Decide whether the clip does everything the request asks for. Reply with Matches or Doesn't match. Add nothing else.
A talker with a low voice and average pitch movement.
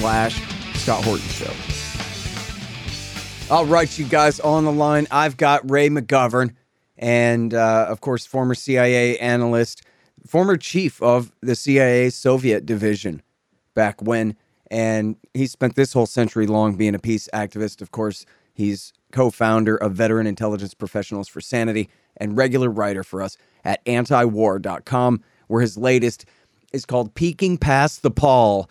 Matches